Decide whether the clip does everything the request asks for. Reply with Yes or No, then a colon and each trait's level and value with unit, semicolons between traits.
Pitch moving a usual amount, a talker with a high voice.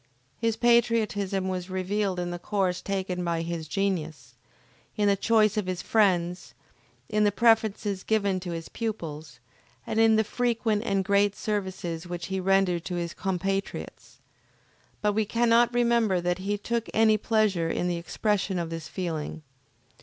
Yes: average, 3.5 semitones; high, 195 Hz